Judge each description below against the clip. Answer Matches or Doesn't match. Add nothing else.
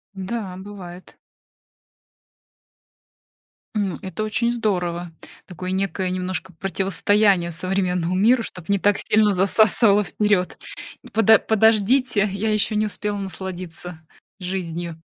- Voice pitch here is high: Matches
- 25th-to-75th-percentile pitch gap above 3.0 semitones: Doesn't match